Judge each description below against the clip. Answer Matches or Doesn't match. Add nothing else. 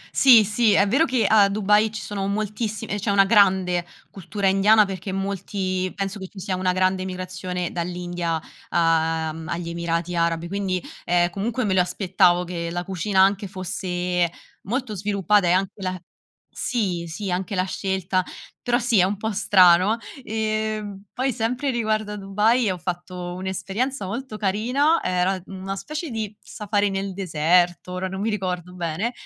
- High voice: Matches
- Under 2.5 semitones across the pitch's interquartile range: Doesn't match